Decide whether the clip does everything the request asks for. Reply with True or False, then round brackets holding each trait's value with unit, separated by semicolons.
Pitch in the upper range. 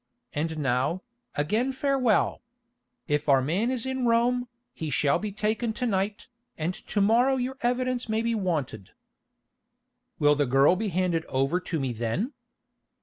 True (195 Hz)